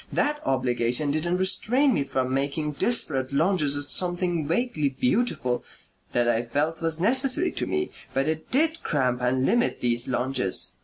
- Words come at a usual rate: Yes, average, 155 wpm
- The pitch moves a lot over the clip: Yes, wide, 6.8 semitones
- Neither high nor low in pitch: Yes, medium, 150 Hz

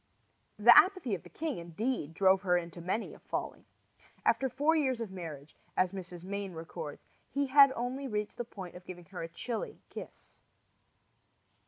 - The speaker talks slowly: No, average, 170 wpm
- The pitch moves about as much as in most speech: No, wide, 6.3 semitones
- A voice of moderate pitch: No, high, 195 Hz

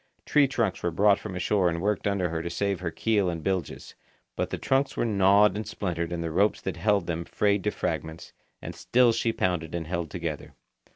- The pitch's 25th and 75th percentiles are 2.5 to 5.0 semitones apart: Yes, average, 3.7 semitones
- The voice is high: No, very low, 95 Hz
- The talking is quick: Yes, fast, 215 wpm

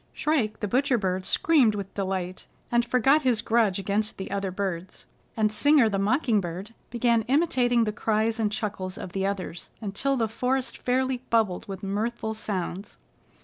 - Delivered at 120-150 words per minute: No, average, 165 wpm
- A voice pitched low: No, high, 215 Hz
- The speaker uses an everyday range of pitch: Yes, average, 3.7 semitones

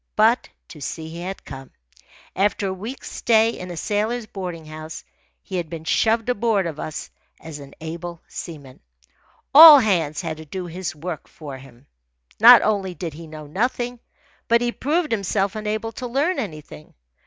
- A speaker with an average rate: Yes, average, 170 wpm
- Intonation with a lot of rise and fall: Yes, wide, 6.1 semitones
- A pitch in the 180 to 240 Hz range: Yes, medium, 185 Hz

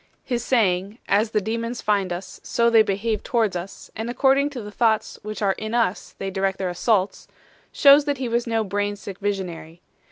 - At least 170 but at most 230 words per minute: Yes, average, 195 wpm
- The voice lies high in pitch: Yes, high, 215 Hz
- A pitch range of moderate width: Yes, average, 3.2 semitones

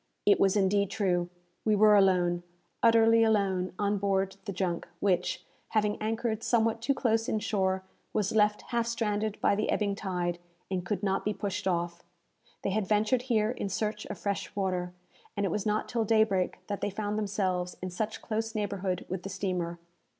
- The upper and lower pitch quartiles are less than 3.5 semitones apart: Yes, narrow, 2.5 semitones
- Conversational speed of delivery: Yes, average, 180 wpm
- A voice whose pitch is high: Yes, high, 205 Hz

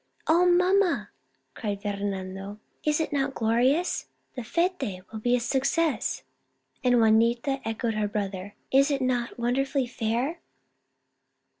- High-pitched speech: Yes, high, 245 Hz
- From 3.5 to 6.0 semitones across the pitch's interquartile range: Yes, average, 4.6 semitones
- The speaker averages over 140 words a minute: No, slow, 135 wpm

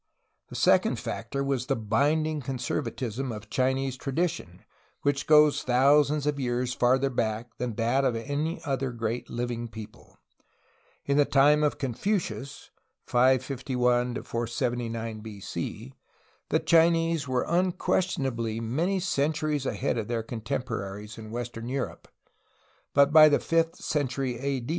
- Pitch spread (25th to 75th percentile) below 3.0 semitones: No, average, 3.7 semitones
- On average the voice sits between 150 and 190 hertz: No, low, 130 Hz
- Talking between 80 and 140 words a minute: Yes, slow, 135 wpm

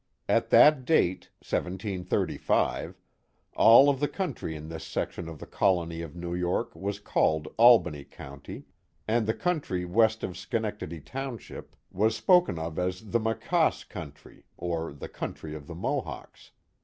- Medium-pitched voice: No, very low, 90 Hz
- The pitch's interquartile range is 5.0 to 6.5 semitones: Yes, wide, 5.6 semitones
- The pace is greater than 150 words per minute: No, average, 145 wpm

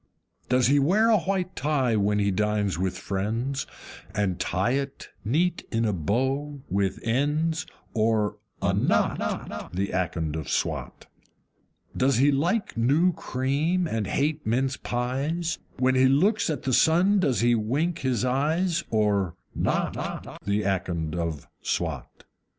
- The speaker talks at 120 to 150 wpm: Yes, average, 140 wpm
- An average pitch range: No, wide, 6.7 semitones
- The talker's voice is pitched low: Yes, low, 130 Hz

